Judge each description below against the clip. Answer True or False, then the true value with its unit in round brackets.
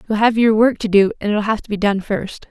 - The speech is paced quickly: True (310 wpm)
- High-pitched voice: True (210 Hz)